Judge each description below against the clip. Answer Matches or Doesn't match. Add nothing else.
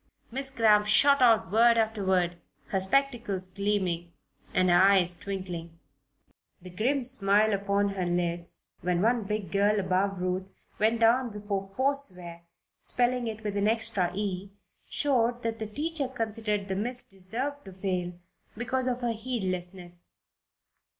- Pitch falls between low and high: Doesn't match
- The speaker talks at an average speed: Matches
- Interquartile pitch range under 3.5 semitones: Doesn't match